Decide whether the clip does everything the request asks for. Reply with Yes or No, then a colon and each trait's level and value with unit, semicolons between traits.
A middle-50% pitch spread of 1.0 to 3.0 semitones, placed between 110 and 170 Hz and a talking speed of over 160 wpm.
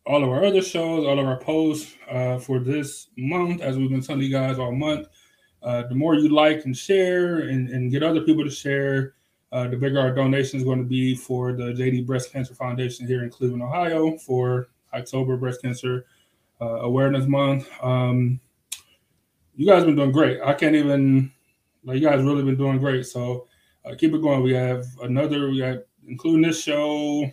Yes: average, 2.7 semitones; low, 135 Hz; average, 200 wpm